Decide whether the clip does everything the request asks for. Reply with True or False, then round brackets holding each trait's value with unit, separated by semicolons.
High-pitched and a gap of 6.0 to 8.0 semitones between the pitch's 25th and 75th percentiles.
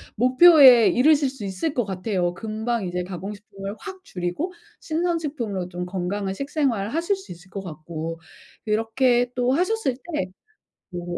True (220 Hz; 7.1 semitones)